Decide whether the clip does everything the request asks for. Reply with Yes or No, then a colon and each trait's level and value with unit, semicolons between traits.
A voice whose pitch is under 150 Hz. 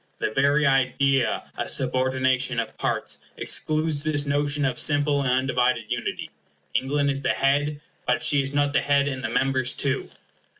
Yes: low, 135 Hz